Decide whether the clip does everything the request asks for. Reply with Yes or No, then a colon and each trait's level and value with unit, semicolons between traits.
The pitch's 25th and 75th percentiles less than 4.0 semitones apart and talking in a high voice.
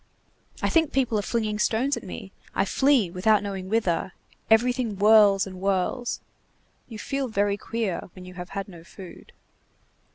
Yes: average, 3.4 semitones; high, 210 Hz